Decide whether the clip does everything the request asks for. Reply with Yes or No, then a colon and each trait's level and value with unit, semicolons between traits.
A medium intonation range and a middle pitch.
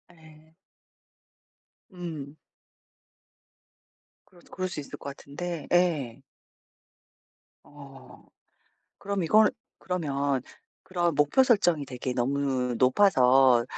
Yes: average, 4.7 semitones; medium, 150 Hz